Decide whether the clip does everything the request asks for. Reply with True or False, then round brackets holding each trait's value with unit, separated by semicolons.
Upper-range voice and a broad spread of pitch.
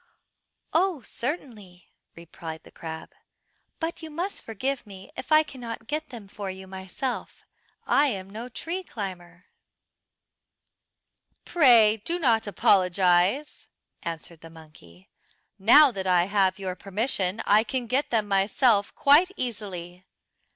True (210 Hz; 6.1 semitones)